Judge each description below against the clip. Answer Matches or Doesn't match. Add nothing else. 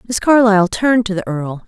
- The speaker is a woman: Matches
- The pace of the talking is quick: Matches